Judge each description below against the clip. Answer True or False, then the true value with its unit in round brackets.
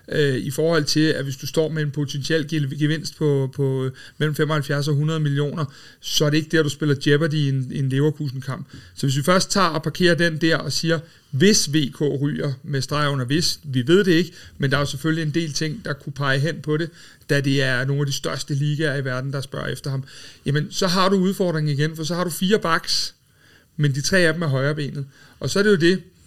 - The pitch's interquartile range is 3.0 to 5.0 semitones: False (2.5 semitones)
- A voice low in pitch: False (150 Hz)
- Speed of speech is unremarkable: False (240 wpm)